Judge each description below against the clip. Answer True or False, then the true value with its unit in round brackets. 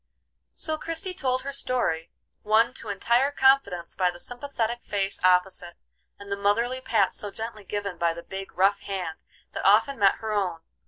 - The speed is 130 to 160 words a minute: False (170 wpm)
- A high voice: True (205 Hz)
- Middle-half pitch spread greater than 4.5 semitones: True (5.0 semitones)